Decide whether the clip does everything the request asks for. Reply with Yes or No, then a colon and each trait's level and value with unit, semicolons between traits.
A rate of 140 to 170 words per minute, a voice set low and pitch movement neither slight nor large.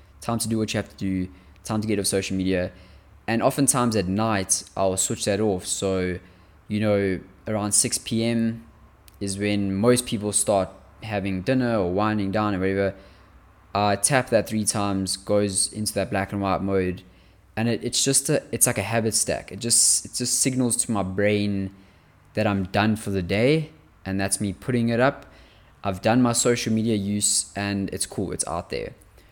No: average, 190 wpm; low, 100 Hz; average, 3.0 semitones